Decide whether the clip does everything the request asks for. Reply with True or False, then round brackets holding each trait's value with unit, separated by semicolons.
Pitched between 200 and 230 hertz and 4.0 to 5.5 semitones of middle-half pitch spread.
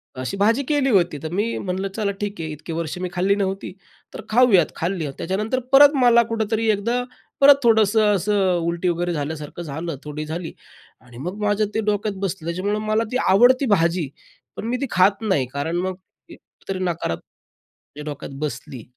False (190 Hz; 4.5 semitones)